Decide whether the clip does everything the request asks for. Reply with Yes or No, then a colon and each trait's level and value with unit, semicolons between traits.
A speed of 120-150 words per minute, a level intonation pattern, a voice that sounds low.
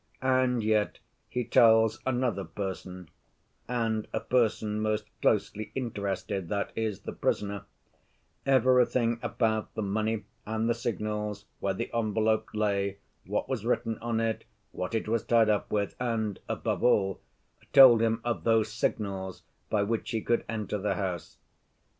Yes: average, 140 wpm; narrow, 2.3 semitones; low, 110 Hz